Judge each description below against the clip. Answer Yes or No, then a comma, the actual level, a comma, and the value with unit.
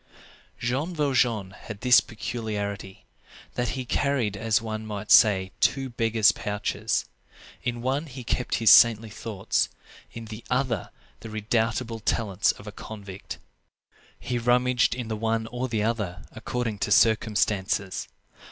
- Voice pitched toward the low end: Yes, low, 115 Hz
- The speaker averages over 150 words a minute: No, slow, 135 wpm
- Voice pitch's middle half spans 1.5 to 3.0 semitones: Yes, average, 2.7 semitones